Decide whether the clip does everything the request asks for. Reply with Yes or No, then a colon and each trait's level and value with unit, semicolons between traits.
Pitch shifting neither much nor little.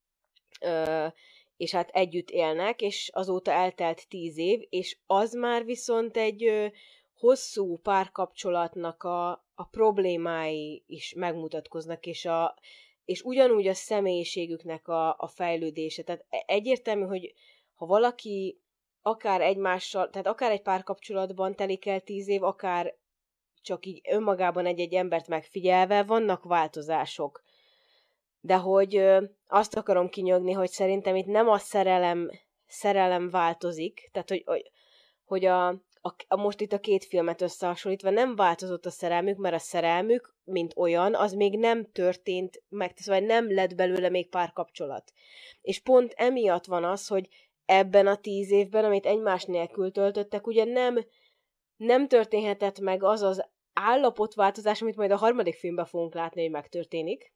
Yes: average, 3.1 semitones